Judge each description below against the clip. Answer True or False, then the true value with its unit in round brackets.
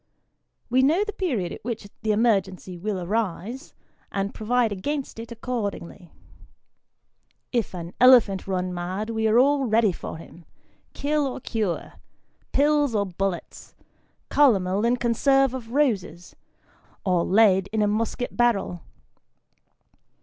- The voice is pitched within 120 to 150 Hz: False (220 Hz)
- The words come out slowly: True (130 wpm)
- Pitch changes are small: False (4.7 semitones)